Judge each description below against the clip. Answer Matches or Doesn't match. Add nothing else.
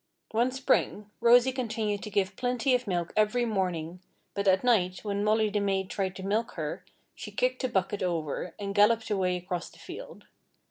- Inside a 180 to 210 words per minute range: Matches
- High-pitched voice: Matches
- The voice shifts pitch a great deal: Doesn't match